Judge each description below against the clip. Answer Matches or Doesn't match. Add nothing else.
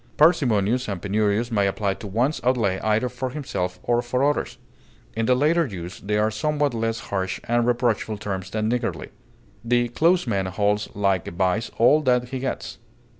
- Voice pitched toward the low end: Matches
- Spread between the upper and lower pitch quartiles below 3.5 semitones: Doesn't match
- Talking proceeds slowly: Doesn't match